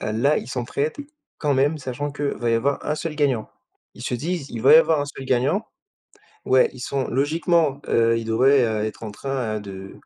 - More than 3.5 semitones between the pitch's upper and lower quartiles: Yes, average, 4.1 semitones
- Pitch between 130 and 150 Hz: Yes, low, 135 Hz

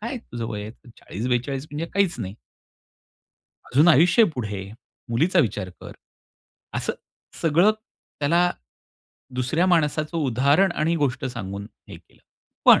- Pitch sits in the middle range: Yes, medium, 145 Hz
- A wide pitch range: Yes, wide, 6.0 semitones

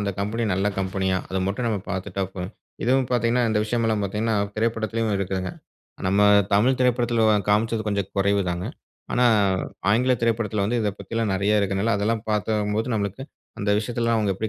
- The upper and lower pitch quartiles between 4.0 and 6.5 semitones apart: No, narrow, 2.4 semitones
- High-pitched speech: No, low, 105 Hz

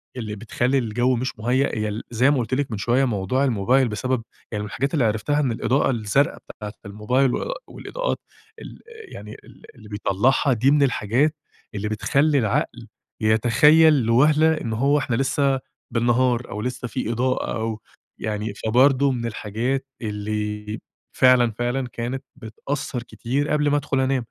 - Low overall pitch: Yes, low, 120 Hz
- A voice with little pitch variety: No, average, 3.8 semitones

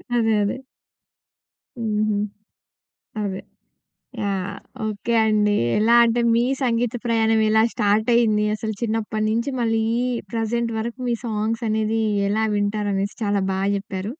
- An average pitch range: No, narrow, 1.7 semitones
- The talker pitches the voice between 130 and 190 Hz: No, high, 220 Hz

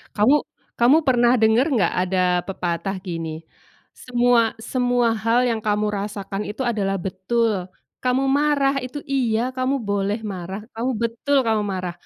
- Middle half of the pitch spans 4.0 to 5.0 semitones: Yes, average, 4.3 semitones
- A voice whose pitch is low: No, high, 225 Hz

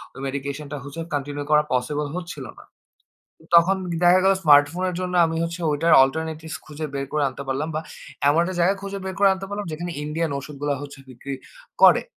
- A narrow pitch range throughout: No, average, 3.4 semitones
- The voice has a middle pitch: Yes, medium, 155 Hz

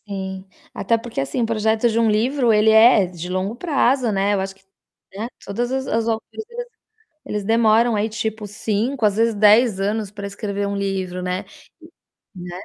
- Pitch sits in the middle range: No, high, 215 Hz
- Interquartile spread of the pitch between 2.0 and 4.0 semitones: Yes, average, 2.7 semitones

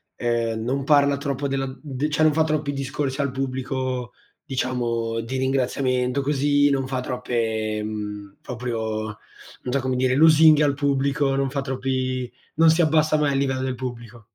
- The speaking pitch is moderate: No, low, 130 Hz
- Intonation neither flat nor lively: No, narrow, 2.3 semitones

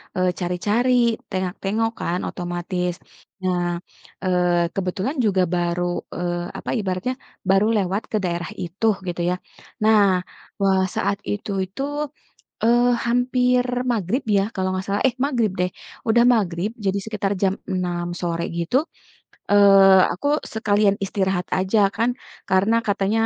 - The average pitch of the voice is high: Yes, high, 195 Hz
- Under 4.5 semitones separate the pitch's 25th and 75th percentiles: Yes, average, 3.3 semitones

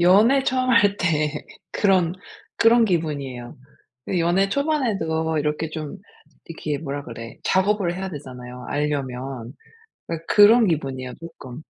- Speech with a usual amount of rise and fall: No, wide, 5.9 semitones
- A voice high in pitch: No, medium, 160 Hz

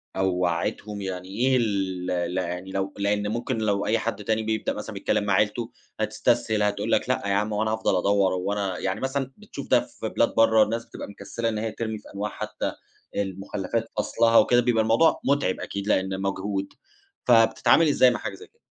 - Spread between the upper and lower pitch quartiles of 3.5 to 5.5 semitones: No, average, 2.7 semitones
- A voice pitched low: Yes, low, 105 Hz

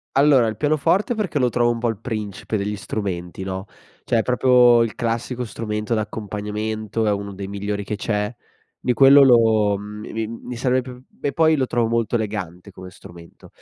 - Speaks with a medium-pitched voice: No, low, 110 Hz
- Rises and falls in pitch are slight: No, average, 3.1 semitones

